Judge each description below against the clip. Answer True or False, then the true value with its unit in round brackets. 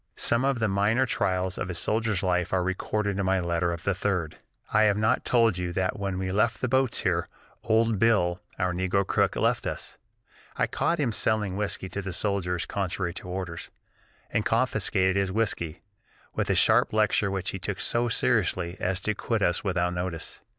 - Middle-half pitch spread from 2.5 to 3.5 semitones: True (3.1 semitones)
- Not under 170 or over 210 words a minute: True (190 wpm)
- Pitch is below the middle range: True (95 Hz)